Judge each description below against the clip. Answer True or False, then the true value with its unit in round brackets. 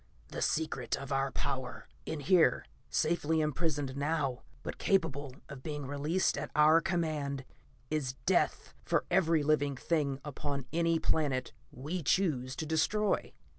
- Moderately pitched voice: True (150 Hz)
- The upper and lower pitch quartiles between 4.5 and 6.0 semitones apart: False (2.7 semitones)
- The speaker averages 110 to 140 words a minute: True (135 wpm)